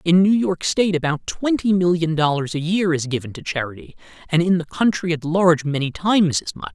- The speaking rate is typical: No, fast, 215 wpm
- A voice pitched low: No, medium, 165 Hz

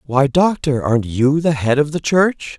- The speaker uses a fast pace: Yes, fast, 210 wpm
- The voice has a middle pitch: Yes, medium, 145 Hz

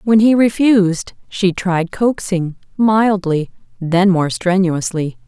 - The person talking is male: No, female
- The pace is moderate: No, slow, 115 wpm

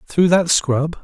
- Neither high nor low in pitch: Yes, medium, 160 Hz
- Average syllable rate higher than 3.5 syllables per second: No, 3.4 syllables/s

